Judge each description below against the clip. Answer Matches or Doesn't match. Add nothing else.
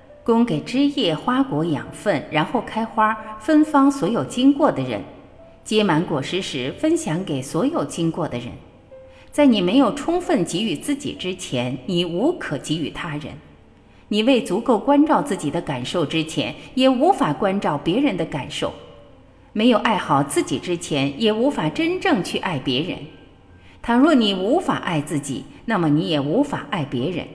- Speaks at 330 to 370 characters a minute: Doesn't match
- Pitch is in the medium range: Doesn't match